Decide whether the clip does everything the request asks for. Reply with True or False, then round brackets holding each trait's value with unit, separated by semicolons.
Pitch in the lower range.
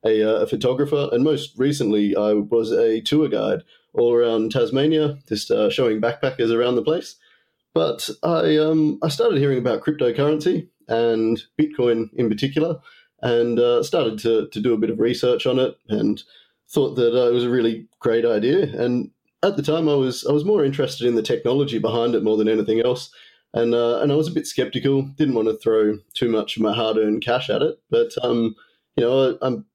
True (120 Hz)